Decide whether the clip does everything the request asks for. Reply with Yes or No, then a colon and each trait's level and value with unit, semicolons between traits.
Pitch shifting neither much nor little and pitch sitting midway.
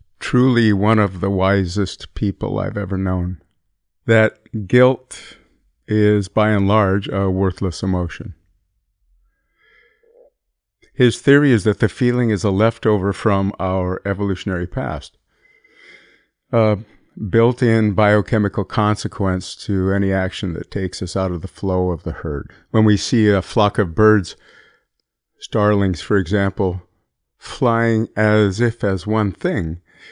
No: average, 3.0 semitones; low, 105 Hz